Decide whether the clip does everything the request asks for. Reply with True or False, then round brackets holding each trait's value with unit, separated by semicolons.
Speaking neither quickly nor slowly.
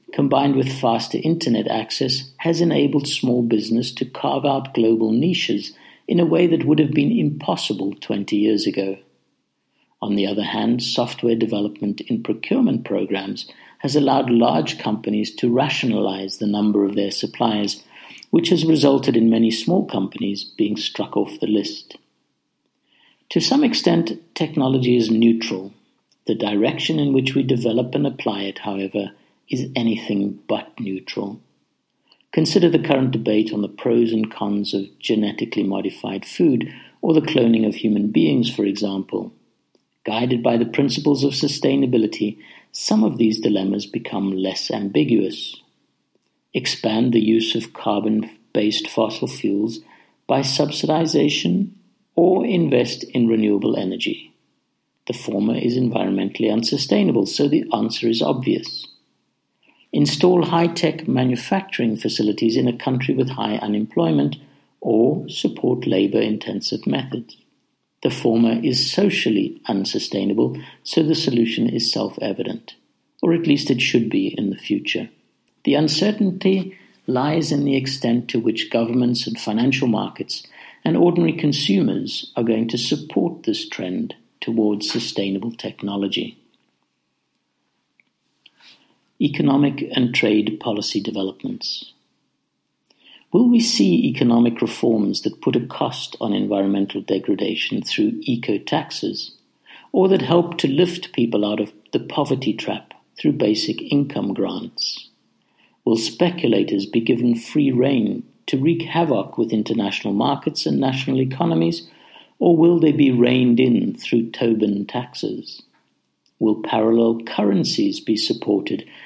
False (130 wpm)